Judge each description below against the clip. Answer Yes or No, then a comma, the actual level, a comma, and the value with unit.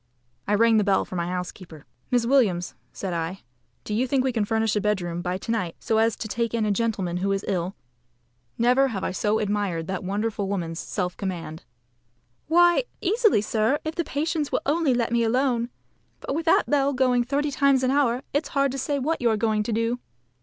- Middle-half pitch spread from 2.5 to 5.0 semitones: No, wide, 5.5 semitones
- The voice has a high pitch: Yes, high, 225 Hz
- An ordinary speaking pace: No, fast, 210 wpm